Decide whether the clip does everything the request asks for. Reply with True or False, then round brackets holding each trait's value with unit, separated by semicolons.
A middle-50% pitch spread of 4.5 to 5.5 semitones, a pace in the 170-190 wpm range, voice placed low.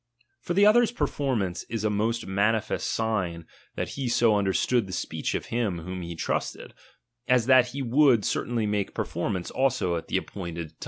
True (5.2 semitones; 175 wpm; 110 Hz)